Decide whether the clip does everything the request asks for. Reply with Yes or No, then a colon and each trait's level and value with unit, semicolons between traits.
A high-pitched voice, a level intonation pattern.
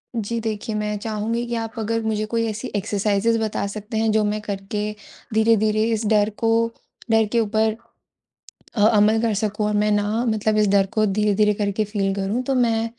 Yes: high, 215 Hz; narrow, 1.3 semitones